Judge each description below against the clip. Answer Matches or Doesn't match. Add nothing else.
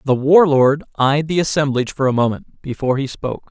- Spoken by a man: Matches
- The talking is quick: Doesn't match